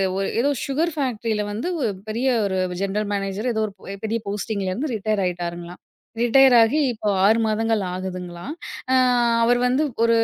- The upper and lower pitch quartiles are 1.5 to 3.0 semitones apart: No, average, 3.7 semitones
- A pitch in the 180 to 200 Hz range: No, high, 215 Hz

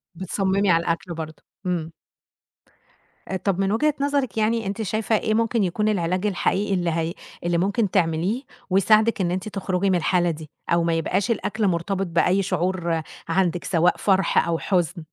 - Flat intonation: No, average, 3.2 semitones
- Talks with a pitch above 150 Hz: Yes, medium, 185 Hz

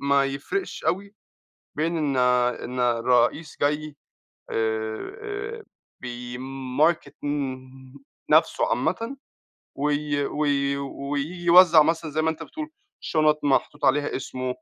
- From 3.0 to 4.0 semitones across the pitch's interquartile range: Yes, average, 3.7 semitones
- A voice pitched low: No, medium, 145 Hz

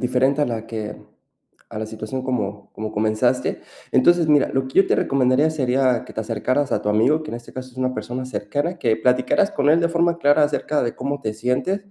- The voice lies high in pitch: No, low, 130 Hz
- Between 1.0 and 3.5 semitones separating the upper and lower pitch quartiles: No, average, 4.3 semitones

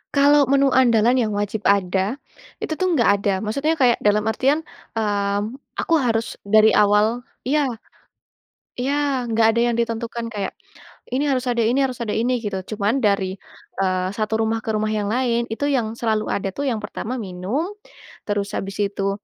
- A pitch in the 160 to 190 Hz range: No, high, 225 Hz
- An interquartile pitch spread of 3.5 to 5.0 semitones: Yes, average, 3.8 semitones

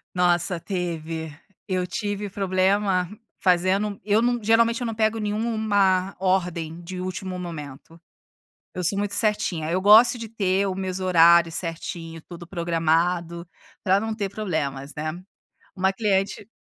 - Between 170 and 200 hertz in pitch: Yes, medium, 185 Hz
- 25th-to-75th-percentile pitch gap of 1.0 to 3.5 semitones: Yes, average, 3.1 semitones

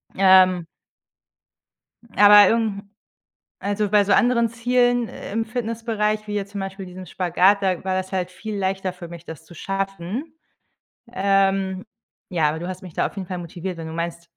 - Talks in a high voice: Yes, high, 195 Hz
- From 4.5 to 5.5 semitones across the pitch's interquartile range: No, narrow, 2.6 semitones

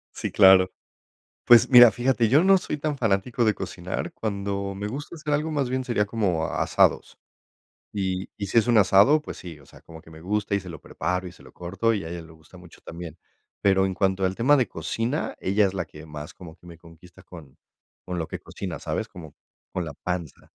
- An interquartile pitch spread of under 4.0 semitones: No, average, 4.9 semitones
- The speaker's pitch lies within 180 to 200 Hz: No, very low, 95 Hz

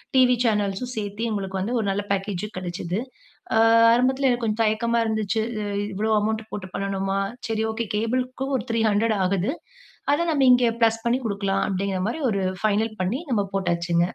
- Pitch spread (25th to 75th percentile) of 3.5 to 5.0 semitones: No, average, 3.0 semitones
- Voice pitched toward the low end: No, high, 215 Hz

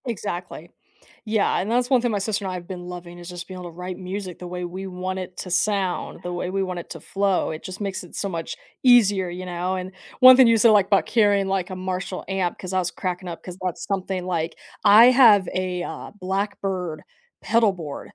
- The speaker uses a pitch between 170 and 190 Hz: Yes, medium, 185 Hz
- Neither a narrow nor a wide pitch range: No, narrow, 2.0 semitones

